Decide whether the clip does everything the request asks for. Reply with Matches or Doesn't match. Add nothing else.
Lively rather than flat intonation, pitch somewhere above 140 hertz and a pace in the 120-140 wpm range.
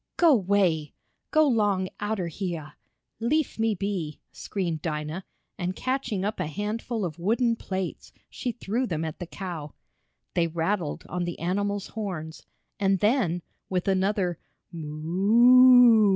Doesn't match